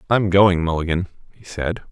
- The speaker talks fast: No, average, 155 wpm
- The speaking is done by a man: Yes, male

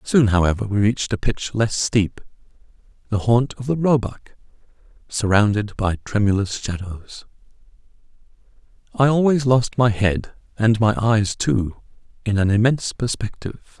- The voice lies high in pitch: No, low, 110 Hz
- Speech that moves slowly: Yes, slow, 130 wpm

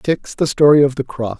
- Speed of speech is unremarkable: No, fast, 260 wpm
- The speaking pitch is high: No, low, 135 Hz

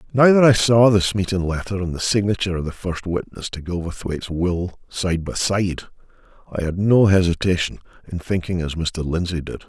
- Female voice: No, male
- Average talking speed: Yes, average, 185 wpm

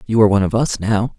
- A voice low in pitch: Yes, low, 105 Hz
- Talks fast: Yes, fast, 305 wpm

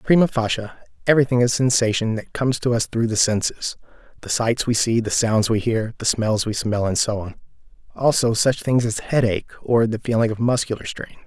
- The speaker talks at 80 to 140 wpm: No, average, 200 wpm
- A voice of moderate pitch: No, low, 115 Hz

